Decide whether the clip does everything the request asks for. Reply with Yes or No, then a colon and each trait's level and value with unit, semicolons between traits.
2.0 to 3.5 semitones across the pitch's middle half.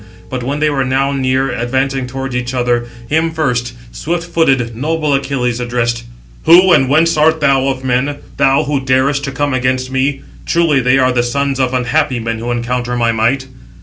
Yes: narrow, 2.5 semitones